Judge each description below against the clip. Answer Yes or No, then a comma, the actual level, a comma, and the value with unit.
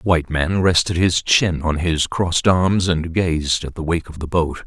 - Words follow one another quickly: Yes, fast, 230 wpm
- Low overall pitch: Yes, very low, 85 Hz